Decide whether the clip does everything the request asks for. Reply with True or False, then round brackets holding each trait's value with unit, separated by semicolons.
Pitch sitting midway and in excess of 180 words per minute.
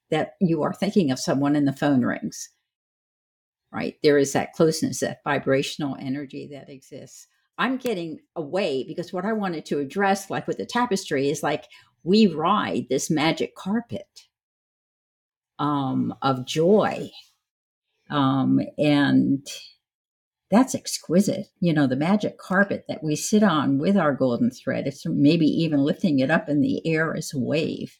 False (160 Hz; 155 wpm)